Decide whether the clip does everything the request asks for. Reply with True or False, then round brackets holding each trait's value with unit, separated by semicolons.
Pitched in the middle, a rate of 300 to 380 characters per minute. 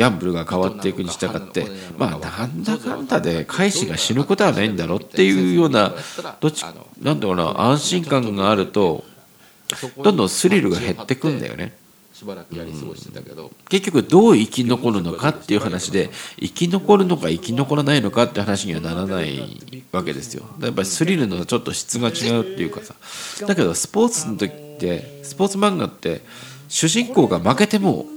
False (130 Hz; 370 characters per minute)